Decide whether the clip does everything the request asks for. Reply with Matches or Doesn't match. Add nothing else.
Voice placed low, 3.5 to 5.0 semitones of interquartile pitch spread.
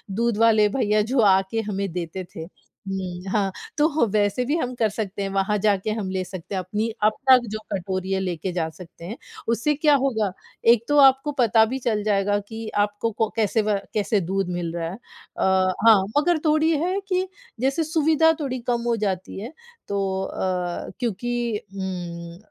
Doesn't match